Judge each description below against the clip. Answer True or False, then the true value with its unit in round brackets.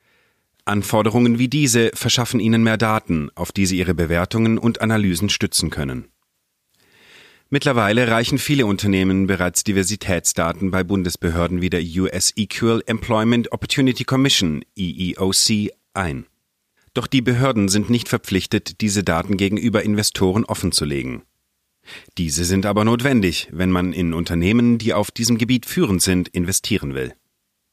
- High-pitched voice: False (105 Hz)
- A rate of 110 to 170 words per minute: True (130 wpm)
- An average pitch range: True (4.3 semitones)